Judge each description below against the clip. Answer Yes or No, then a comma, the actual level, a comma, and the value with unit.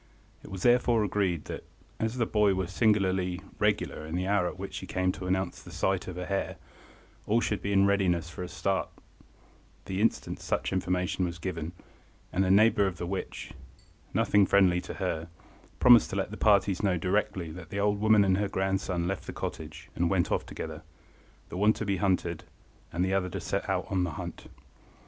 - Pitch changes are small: Yes, narrow, 2.0 semitones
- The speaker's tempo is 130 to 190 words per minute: No, average, 200 wpm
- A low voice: Yes, very low, 95 Hz